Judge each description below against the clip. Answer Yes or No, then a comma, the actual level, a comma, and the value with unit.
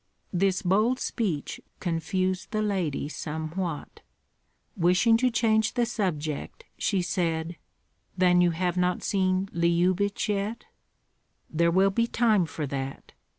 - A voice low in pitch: No, medium, 185 Hz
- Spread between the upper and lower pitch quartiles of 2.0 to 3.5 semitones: Yes, average, 3.2 semitones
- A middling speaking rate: No, slow, 120 wpm